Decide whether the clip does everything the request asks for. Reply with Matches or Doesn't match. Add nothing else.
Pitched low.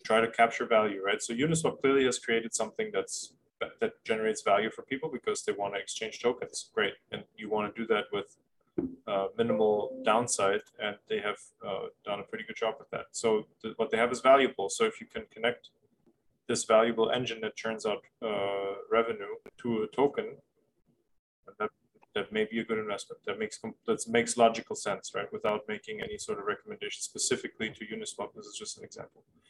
Matches